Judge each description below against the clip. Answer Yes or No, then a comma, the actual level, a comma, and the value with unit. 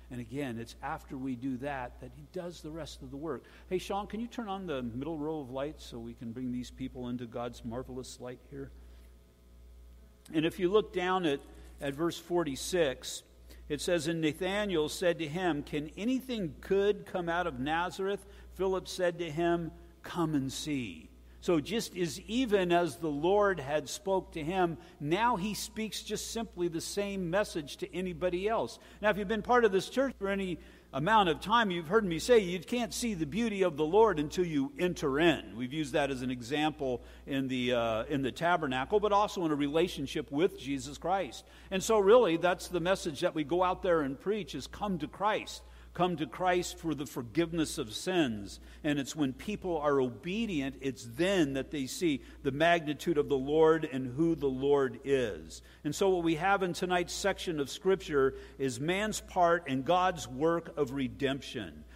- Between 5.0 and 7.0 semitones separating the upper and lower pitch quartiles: Yes, wide, 5.4 semitones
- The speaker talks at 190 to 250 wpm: Yes, average, 195 wpm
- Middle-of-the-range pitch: Yes, medium, 165 Hz